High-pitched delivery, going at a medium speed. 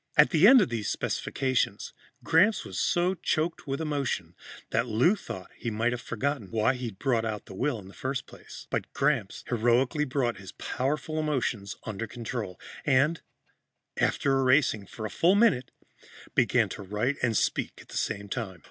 No: low, 125 Hz; average, 175 wpm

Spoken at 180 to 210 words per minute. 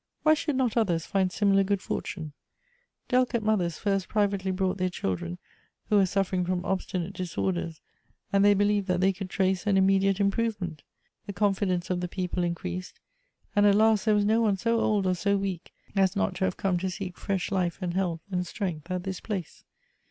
Yes: average, 195 wpm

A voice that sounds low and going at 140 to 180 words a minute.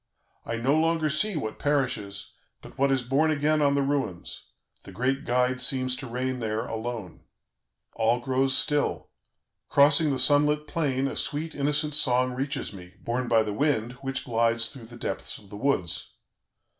Yes: low, 130 Hz; average, 170 wpm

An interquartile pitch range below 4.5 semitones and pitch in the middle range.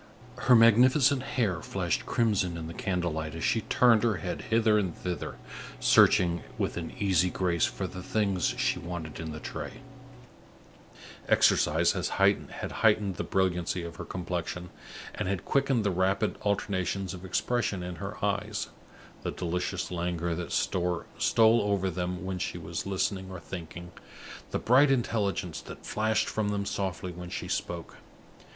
No: average, 3.5 semitones; very low, 95 Hz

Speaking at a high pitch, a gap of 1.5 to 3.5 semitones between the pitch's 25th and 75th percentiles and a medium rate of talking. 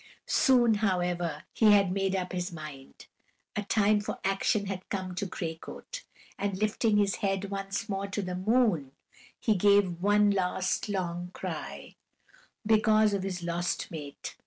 Yes: high, 195 Hz; narrow, 2.6 semitones; average, 155 wpm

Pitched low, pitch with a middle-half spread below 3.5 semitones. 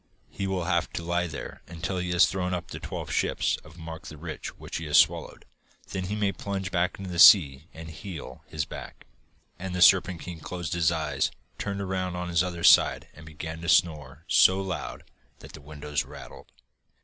Yes: very low, 85 Hz; narrow, 2.6 semitones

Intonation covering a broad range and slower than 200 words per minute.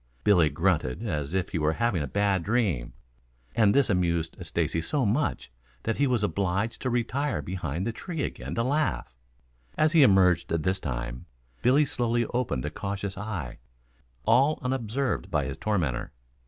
Yes: wide, 6.6 semitones; average, 160 wpm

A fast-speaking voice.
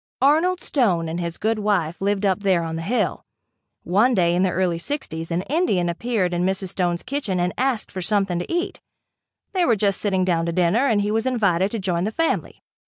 Yes: fast, 215 wpm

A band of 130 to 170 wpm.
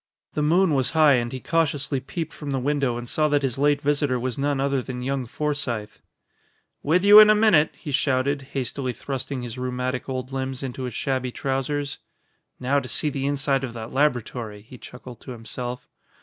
No: average, 190 wpm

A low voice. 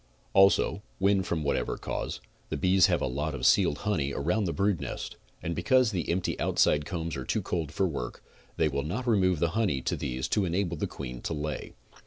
Yes: very low, 85 Hz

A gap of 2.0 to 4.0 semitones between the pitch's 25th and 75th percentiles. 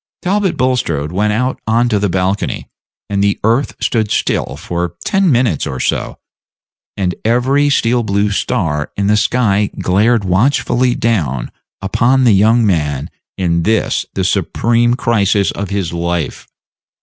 No: average, 4.6 semitones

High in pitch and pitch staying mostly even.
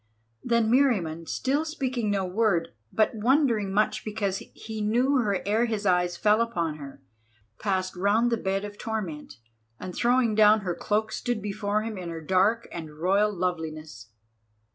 No: high, 210 Hz; average, 3.9 semitones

